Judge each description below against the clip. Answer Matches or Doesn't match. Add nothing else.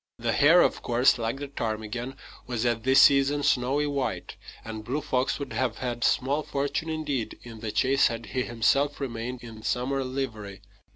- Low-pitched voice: Matches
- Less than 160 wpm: Doesn't match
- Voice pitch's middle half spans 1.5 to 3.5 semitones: Matches